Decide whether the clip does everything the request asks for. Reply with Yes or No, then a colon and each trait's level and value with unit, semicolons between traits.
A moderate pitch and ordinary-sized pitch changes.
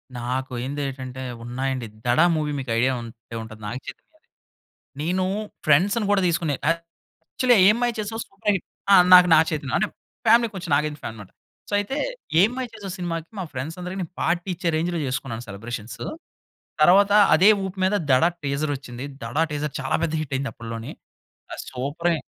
No: medium, 155 Hz; wide, 6.2 semitones